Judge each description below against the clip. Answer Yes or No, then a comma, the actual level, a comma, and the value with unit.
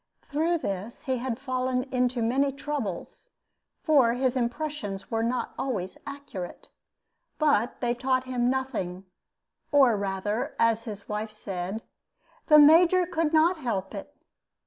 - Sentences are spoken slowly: Yes, slow, 130 wpm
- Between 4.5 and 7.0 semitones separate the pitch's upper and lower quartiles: Yes, average, 5.0 semitones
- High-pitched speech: Yes, very high, 250 Hz